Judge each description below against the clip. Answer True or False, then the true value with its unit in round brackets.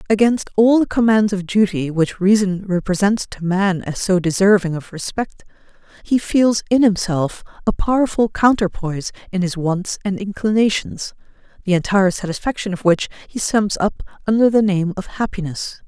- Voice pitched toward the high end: True (200 Hz)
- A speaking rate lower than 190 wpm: True (155 wpm)